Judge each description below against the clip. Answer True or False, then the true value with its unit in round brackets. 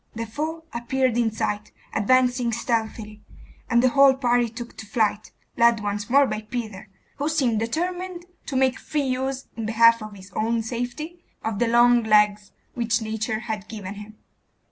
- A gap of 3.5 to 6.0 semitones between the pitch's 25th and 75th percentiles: False (3.0 semitones)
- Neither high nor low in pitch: False (235 Hz)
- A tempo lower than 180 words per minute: True (165 wpm)